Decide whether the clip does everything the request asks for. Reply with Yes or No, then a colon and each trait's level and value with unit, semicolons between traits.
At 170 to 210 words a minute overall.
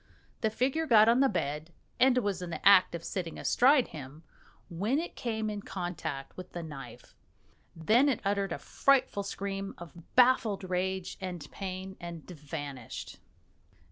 No: average, 155 wpm